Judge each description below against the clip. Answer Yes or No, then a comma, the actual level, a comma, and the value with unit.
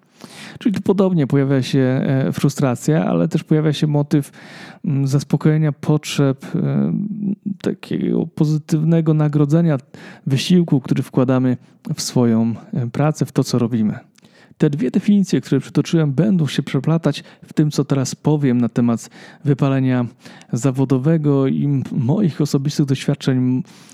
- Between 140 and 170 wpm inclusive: No, average, 115 wpm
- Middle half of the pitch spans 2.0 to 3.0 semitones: No, average, 3.6 semitones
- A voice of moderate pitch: Yes, medium, 150 Hz